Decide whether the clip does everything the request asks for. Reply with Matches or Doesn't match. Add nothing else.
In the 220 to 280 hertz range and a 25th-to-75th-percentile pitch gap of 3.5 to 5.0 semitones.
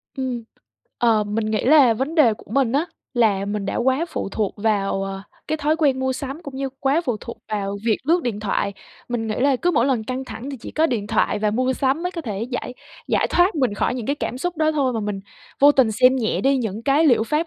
Matches